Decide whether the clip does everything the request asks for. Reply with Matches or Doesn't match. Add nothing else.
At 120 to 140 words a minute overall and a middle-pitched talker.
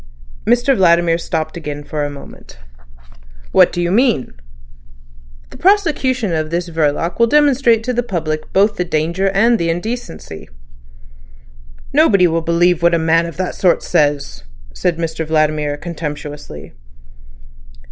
Matches